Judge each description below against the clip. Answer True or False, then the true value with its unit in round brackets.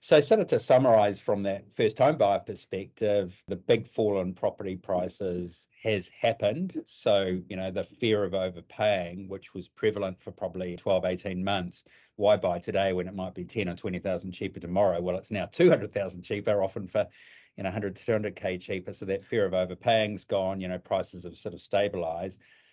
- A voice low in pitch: True (95 Hz)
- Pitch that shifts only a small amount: True (1.7 semitones)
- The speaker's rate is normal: True (190 wpm)